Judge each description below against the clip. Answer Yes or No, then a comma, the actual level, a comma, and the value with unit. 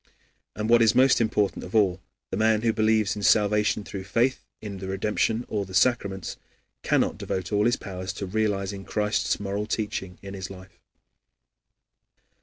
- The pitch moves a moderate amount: No, narrow, 2.2 semitones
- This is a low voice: Yes, low, 105 Hz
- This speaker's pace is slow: No, average, 165 wpm